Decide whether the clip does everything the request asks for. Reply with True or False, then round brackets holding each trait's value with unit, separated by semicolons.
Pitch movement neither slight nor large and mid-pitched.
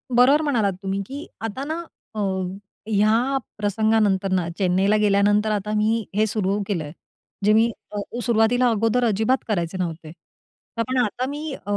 False (3.3 semitones; 215 Hz)